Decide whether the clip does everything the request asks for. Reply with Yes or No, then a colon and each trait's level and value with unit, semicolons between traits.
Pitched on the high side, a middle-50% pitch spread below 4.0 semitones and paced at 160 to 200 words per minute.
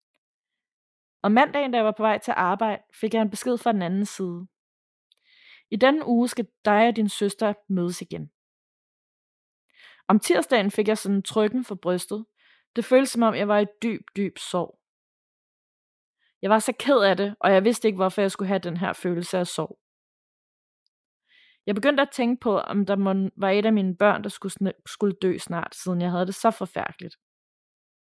Yes: high, 205 Hz; average, 3.3 semitones; average, 185 wpm